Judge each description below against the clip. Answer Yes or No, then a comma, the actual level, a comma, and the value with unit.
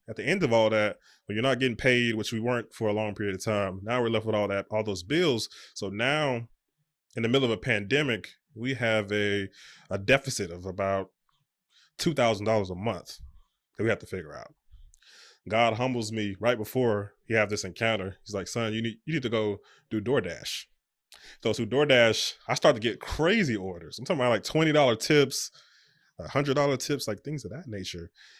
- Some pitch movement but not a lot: Yes, average, 3.7 semitones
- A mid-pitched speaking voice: No, low, 110 Hz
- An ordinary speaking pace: No, fast, 210 wpm